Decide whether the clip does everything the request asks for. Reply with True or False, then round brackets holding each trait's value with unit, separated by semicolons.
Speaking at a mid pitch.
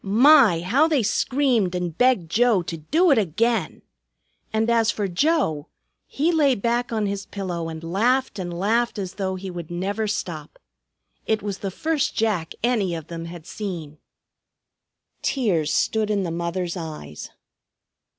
False (200 Hz)